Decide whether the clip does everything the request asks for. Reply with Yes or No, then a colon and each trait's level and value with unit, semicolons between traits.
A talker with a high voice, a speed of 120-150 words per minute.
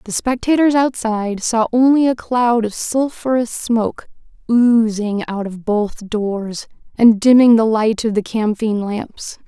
Yes: high, 225 Hz; average, 145 wpm